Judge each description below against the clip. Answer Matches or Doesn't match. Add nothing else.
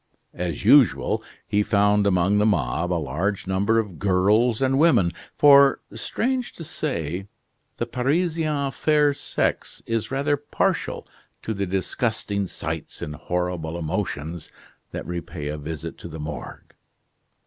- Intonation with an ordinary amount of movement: Doesn't match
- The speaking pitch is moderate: Doesn't match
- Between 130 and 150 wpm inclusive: Matches